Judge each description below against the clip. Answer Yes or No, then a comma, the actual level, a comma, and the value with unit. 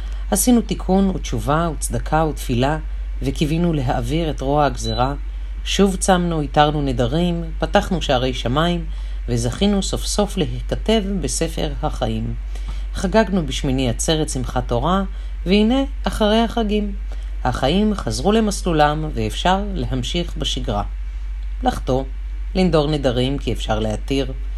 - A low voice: No, medium, 150 Hz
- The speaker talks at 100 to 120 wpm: Yes, average, 105 wpm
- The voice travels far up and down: Yes, wide, 7.0 semitones